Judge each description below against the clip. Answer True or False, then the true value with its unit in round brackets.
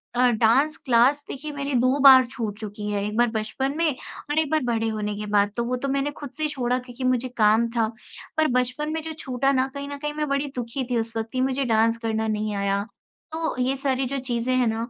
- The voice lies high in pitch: True (250 Hz)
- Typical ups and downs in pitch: True (3.7 semitones)